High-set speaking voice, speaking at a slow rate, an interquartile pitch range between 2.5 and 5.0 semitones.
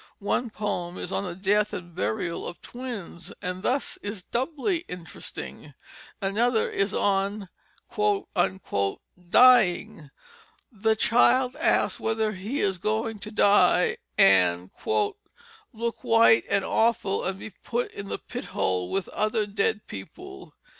Yes: high, 205 Hz; slow, 125 wpm; average, 4.2 semitones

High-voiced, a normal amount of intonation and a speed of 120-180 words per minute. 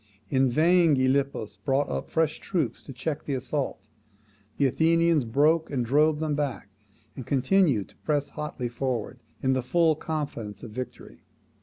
No: medium, 140 Hz; average, 3.5 semitones; average, 155 wpm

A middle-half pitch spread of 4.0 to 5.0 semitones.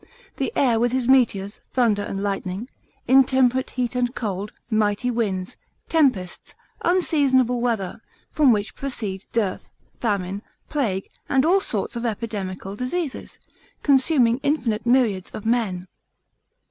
Yes: average, 4.3 semitones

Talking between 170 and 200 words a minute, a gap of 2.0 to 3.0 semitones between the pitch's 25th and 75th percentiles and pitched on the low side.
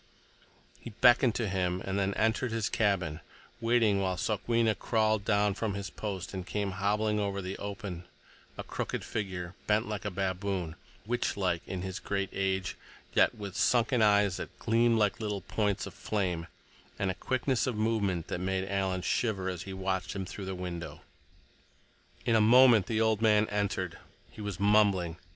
Yes: average, 175 wpm; narrow, 2.6 semitones; low, 100 Hz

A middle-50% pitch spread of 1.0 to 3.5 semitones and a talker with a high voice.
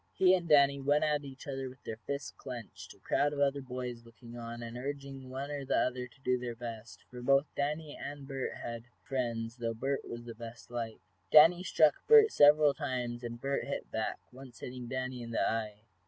No: average, 3.0 semitones; low, 130 Hz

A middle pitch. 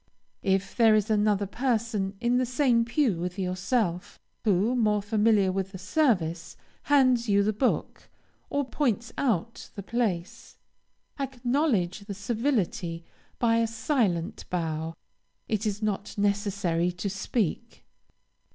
No: high, 210 Hz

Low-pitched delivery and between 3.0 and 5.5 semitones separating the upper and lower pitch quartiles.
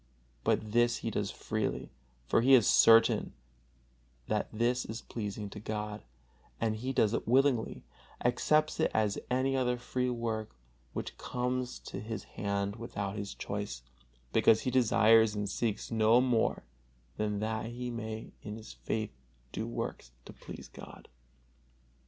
No: low, 110 Hz; narrow, 2.5 semitones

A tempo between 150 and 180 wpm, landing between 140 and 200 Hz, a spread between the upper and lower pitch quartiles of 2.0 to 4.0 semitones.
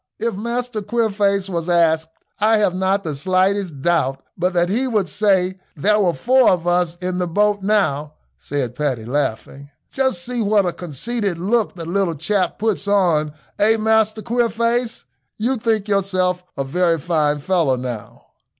No: average, 160 wpm; medium, 185 Hz; average, 4.4 semitones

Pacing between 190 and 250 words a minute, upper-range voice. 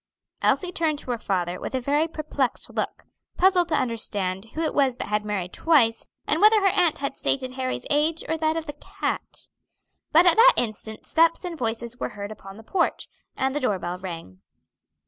Yes: average, 200 wpm; very high, 265 Hz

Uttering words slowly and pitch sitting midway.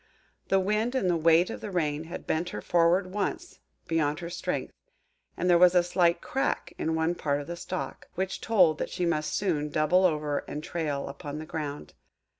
No: average, 195 wpm; medium, 170 Hz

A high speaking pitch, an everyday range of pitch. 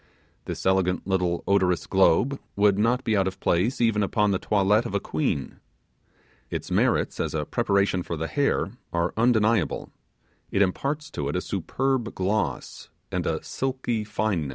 No: low, 100 Hz; average, 3.9 semitones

